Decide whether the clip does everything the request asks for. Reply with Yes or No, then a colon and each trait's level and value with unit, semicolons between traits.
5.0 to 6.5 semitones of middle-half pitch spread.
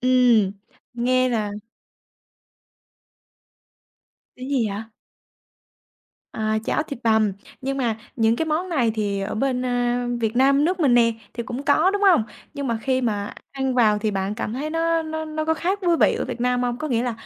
No: average, 4.6 semitones